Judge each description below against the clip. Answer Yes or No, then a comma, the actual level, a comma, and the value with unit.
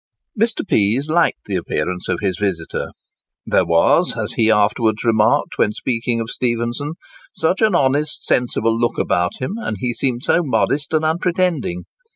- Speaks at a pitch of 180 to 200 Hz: No, low, 120 Hz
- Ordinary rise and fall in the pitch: No, wide, 6.1 semitones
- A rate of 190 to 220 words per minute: No, average, 160 wpm